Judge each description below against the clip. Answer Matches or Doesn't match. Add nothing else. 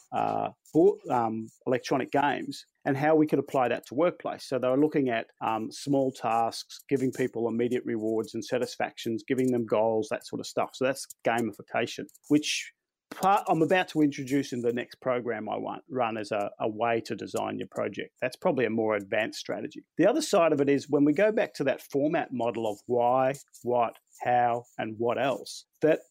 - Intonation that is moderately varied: Matches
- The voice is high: Doesn't match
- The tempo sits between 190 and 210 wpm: Matches